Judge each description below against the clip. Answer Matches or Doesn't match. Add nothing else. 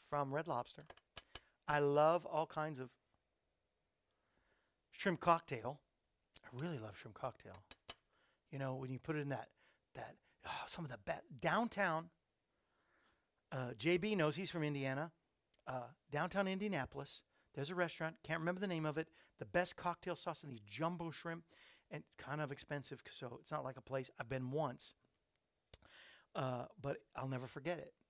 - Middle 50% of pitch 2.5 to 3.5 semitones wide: Doesn't match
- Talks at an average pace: Matches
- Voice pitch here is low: Doesn't match